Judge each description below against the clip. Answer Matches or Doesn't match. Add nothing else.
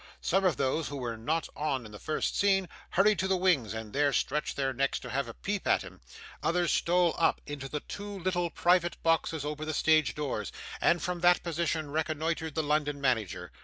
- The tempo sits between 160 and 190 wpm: Doesn't match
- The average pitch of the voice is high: Doesn't match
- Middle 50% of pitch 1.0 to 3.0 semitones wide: Doesn't match